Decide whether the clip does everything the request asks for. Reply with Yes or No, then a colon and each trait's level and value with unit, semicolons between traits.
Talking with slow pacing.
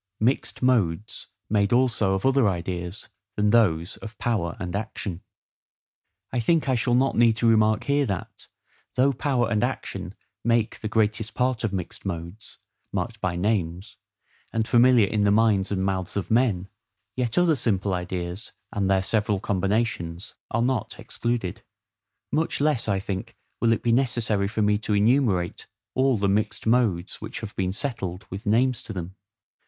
No: average, 165 wpm